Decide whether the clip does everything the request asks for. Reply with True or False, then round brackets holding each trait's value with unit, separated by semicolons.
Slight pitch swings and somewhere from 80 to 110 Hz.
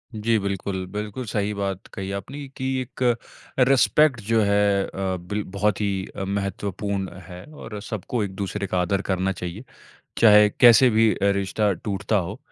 True (2.1 semitones; 100 Hz)